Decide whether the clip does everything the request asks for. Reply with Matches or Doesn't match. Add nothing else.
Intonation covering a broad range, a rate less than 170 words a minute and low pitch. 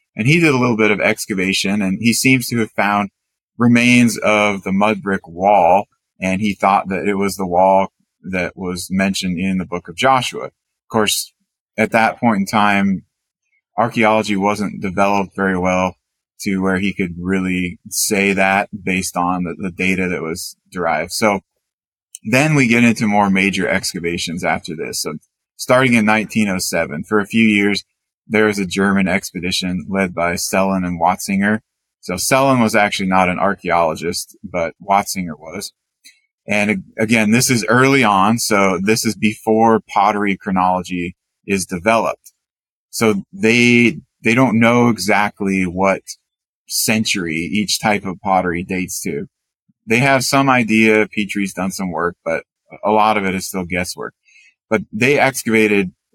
Doesn't match